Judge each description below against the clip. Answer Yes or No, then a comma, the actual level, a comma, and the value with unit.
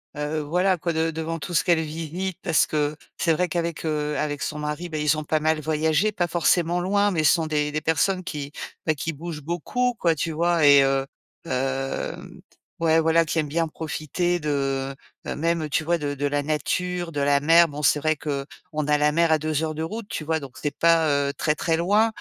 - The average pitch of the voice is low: No, medium, 160 Hz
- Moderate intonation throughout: No, narrow, 2.3 semitones